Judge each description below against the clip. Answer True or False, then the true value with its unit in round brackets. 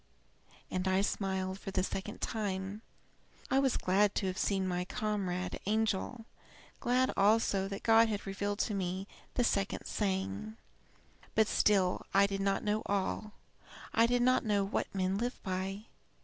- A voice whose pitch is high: True (200 Hz)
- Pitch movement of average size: False (2.2 semitones)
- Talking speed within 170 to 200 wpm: False (155 wpm)